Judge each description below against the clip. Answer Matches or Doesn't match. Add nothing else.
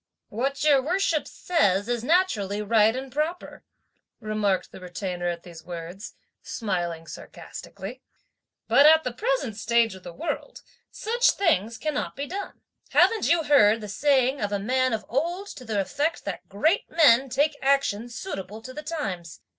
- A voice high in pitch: Matches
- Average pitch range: Doesn't match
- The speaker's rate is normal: Matches